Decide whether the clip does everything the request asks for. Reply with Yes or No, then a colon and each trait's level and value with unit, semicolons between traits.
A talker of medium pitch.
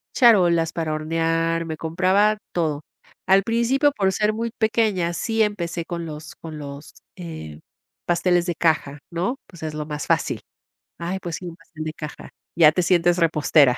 Yes: medium, 170 Hz